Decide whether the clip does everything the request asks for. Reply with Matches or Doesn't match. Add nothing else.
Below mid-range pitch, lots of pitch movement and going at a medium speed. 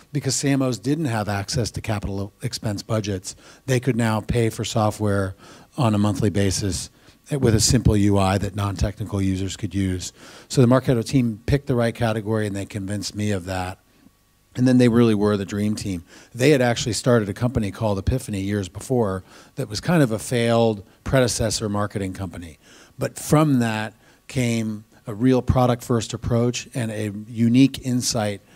Doesn't match